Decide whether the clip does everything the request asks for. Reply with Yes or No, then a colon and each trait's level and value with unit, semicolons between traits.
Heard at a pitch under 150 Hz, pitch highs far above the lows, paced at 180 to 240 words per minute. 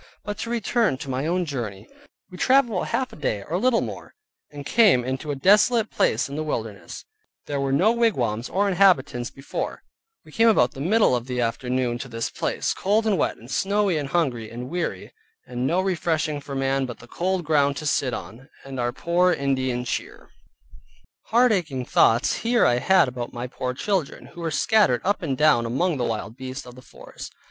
Yes: medium, 140 Hz; wide, 7.2 semitones; fast, 205 wpm